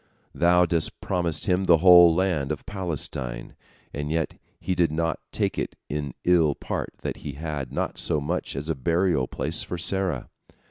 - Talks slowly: No, average, 175 wpm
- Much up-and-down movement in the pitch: No, average, 3.3 semitones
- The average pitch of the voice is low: Yes, very low, 80 Hz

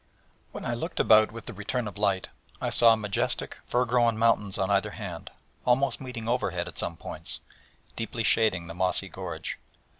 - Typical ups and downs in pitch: Yes, average, 3.2 semitones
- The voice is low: Yes, low, 110 Hz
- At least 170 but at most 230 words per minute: Yes, average, 175 wpm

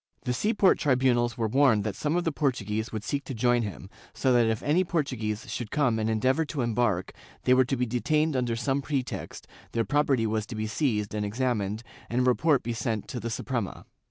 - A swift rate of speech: Yes, fast, 215 wpm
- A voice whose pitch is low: Yes, low, 120 Hz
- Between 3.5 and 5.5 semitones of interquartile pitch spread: Yes, average, 3.9 semitones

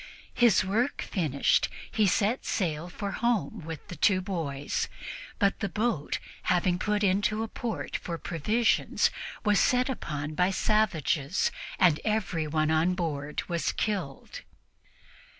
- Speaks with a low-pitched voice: No, medium, 185 Hz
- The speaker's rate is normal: No, slow, 130 wpm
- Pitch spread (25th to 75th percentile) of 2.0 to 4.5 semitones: No, average, 5.0 semitones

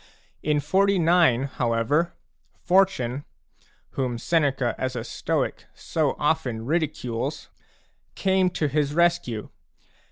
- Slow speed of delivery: Yes, slow, 95 wpm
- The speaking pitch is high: No, medium, 145 Hz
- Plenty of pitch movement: Yes, wide, 5.7 semitones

